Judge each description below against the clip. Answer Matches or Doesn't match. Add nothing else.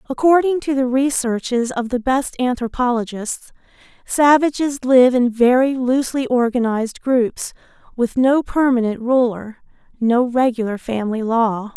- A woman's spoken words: Matches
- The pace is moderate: Doesn't match